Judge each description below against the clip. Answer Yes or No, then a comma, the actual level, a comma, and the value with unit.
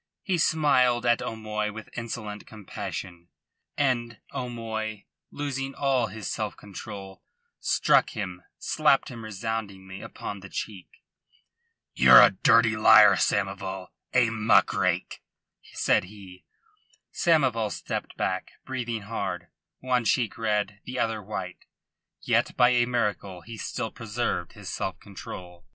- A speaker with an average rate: No, slow, 125 wpm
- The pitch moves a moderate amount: Yes, average, 3.4 semitones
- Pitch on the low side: Yes, low, 110 Hz